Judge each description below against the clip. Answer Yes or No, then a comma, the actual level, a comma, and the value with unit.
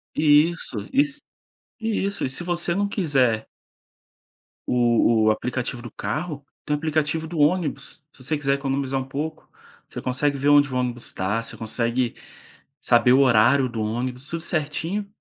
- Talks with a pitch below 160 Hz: Yes, medium, 140 Hz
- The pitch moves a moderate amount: Yes, average, 4.4 semitones